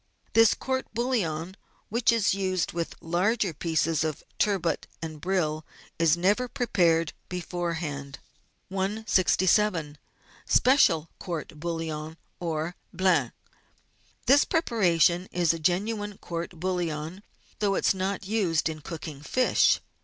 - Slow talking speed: Yes, slow, 115 wpm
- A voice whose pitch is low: No, medium, 175 Hz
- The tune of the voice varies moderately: Yes, average, 3.9 semitones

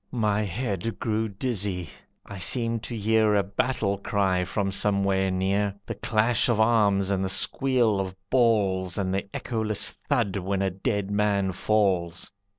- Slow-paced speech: No, average, 155 wpm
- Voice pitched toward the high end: No, low, 100 Hz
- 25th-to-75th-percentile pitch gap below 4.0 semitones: Yes, narrow, 2.4 semitones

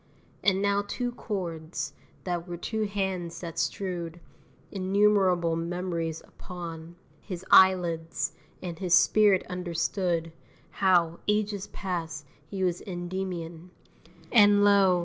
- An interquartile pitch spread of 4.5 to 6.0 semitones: No, narrow, 2.6 semitones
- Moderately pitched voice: Yes, medium, 180 Hz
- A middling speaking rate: No, slow, 110 wpm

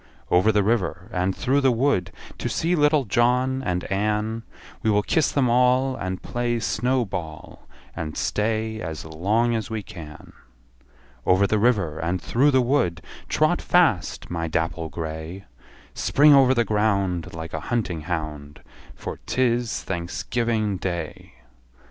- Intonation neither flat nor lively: No, wide, 5.9 semitones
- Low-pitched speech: Yes, low, 105 Hz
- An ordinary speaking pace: Yes, average, 150 wpm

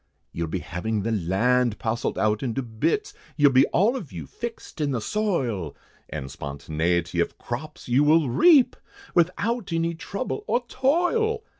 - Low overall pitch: Yes, low, 130 Hz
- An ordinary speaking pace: Yes, average, 155 wpm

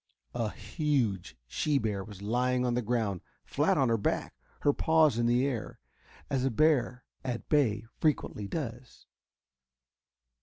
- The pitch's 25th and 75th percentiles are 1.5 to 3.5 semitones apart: No, average, 4.0 semitones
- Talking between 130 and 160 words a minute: Yes, average, 145 wpm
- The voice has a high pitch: No, low, 120 Hz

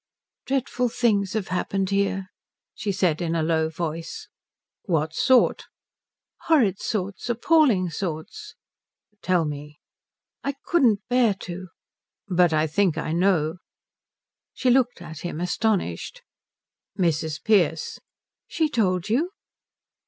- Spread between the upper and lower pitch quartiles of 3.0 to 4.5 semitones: No, wide, 5.5 semitones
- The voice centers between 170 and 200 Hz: Yes, medium, 185 Hz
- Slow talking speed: Yes, slow, 115 wpm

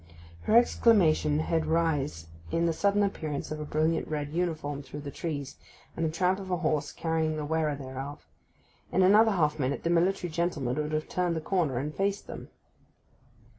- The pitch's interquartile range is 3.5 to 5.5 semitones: No, average, 3.1 semitones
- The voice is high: No, medium, 160 Hz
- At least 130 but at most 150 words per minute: No, average, 180 wpm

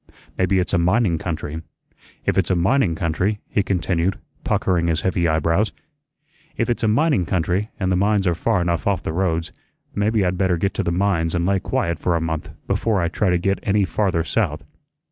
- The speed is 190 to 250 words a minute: Yes, average, 200 wpm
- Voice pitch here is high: No, very low, 90 Hz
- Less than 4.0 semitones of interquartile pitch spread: Yes, average, 2.9 semitones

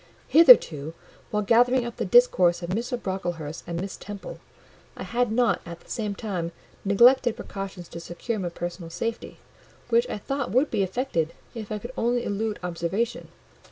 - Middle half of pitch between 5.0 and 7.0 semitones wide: Yes, wide, 5.5 semitones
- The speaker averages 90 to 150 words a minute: No, average, 165 wpm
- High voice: Yes, high, 205 Hz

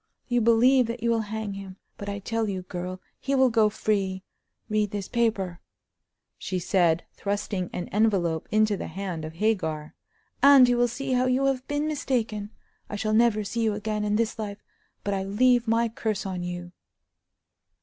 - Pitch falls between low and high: No, high, 215 Hz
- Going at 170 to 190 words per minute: Yes, average, 180 wpm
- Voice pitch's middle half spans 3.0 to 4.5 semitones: Yes, average, 3.4 semitones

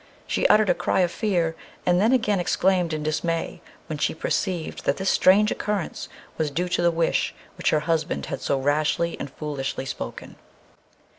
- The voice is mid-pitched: Yes, medium, 170 Hz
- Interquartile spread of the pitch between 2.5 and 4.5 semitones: Yes, average, 3.4 semitones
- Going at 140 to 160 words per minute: No, average, 175 wpm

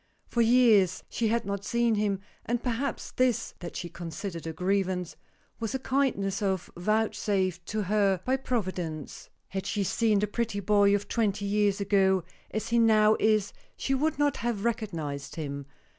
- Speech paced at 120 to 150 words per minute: No, average, 160 wpm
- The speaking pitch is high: Yes, high, 205 Hz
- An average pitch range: Yes, average, 3.5 semitones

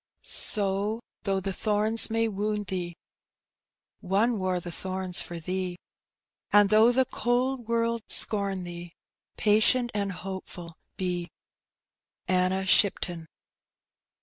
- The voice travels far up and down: No, average, 3.2 semitones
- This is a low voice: No, high, 195 Hz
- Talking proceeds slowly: Yes, slow, 110 wpm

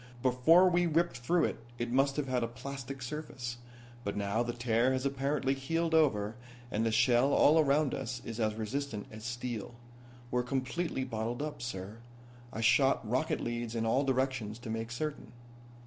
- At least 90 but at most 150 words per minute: No, average, 175 wpm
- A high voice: No, low, 125 Hz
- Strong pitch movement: No, average, 3.2 semitones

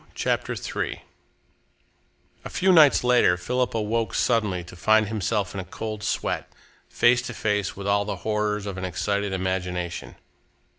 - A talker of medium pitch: No, low, 105 Hz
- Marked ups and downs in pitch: No, average, 3.1 semitones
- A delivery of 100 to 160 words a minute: Yes, average, 150 wpm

